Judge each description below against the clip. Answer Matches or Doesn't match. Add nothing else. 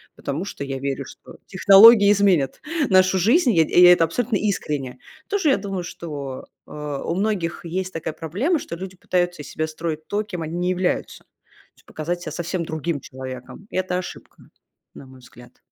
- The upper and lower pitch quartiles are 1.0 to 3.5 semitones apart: Doesn't match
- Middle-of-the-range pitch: Matches